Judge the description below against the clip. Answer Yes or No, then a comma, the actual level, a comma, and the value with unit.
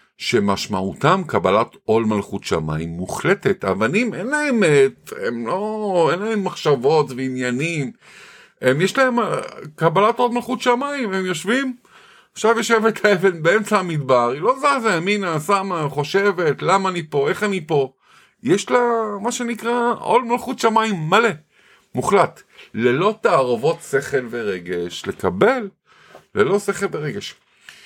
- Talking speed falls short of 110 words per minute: No, average, 125 wpm